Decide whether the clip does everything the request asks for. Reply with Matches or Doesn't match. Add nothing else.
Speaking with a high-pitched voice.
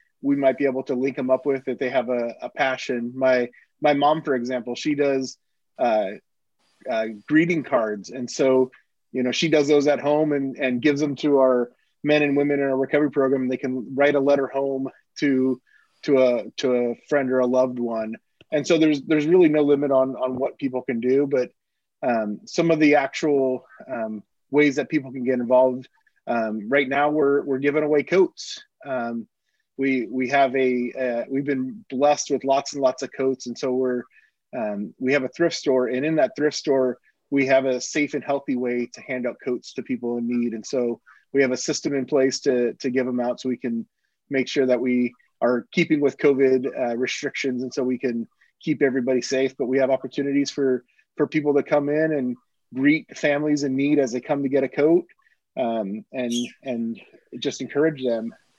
Doesn't match